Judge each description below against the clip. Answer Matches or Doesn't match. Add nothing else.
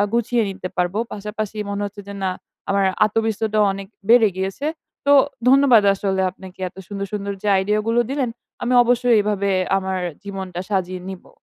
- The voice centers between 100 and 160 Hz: Doesn't match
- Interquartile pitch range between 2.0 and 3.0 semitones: Matches